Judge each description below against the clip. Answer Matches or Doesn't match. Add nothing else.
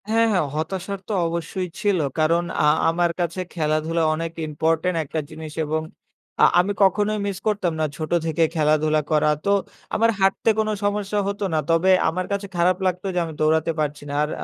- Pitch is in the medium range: Matches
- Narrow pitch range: Doesn't match